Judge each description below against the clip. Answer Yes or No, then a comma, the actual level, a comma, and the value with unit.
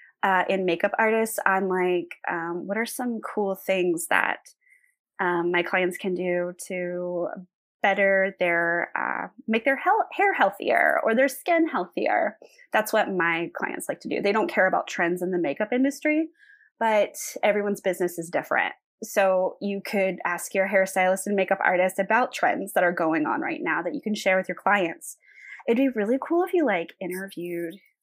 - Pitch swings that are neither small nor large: No, wide, 6.5 semitones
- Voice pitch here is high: Yes, high, 195 Hz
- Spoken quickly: No, average, 180 wpm